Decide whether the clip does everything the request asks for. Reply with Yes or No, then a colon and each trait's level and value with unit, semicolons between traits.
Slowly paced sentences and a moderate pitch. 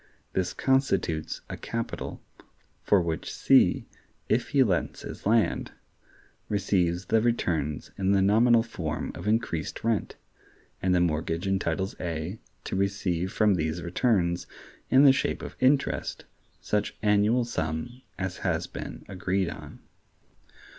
No: slow, 130 wpm; very low, 95 Hz